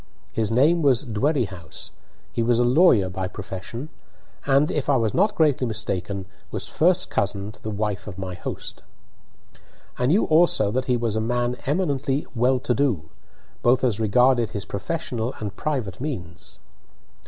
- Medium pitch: No, low, 120 Hz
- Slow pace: No, average, 160 wpm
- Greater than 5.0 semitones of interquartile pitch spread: Yes, wide, 5.4 semitones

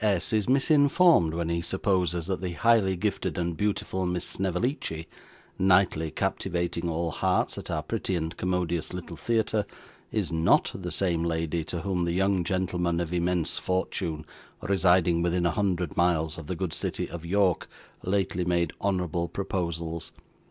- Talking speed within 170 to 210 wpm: No, average, 155 wpm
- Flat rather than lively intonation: Yes, narrow, 2.2 semitones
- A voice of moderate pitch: No, very low, 90 Hz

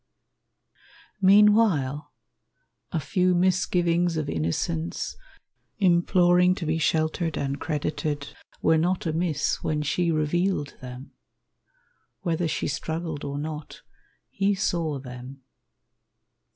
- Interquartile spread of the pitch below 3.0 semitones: No, average, 3.4 semitones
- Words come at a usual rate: No, slow, 100 wpm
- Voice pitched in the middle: Yes, medium, 160 Hz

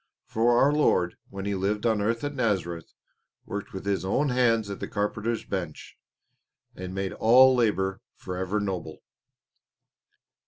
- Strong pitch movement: No, average, 3.5 semitones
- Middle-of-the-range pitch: No, low, 105 Hz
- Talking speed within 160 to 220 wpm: No, average, 145 wpm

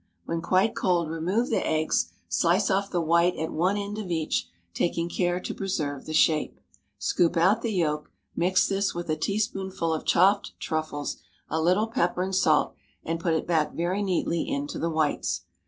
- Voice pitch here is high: No, medium, 175 Hz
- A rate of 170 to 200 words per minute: Yes, average, 180 wpm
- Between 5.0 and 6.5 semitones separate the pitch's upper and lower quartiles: No, average, 3.2 semitones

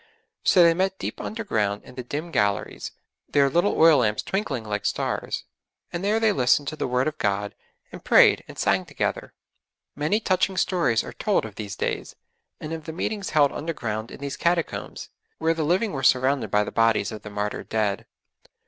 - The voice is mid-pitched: Yes, medium, 145 Hz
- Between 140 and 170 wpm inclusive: No, average, 190 wpm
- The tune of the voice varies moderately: No, wide, 7.8 semitones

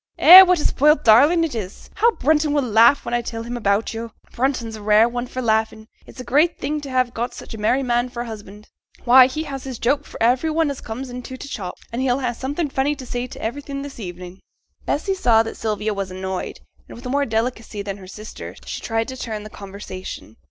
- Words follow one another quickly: Yes, fast, 235 wpm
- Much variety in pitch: No, average, 3.9 semitones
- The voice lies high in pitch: Yes, high, 240 Hz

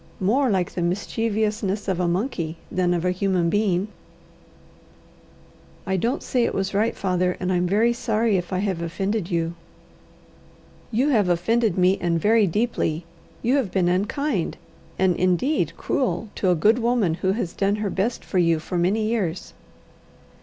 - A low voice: No, high, 190 Hz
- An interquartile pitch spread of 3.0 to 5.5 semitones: Yes, average, 4.0 semitones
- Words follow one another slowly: No, average, 165 wpm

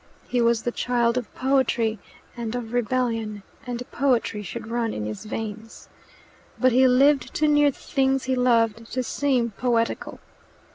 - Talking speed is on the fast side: No, average, 155 wpm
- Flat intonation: Yes, narrow, 2.3 semitones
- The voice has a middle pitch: No, high, 240 Hz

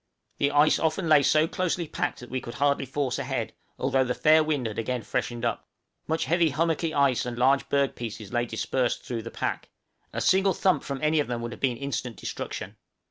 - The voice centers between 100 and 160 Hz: Yes, medium, 140 Hz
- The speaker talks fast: Yes, fast, 210 wpm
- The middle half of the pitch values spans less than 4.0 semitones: No, average, 4.3 semitones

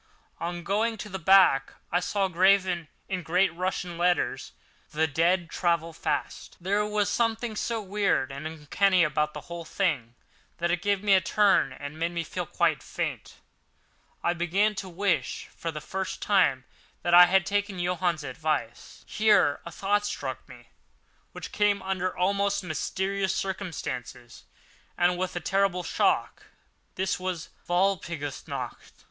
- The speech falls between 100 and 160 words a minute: Yes, average, 150 wpm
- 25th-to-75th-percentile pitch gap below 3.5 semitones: Yes, average, 2.9 semitones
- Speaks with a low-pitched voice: No, medium, 180 Hz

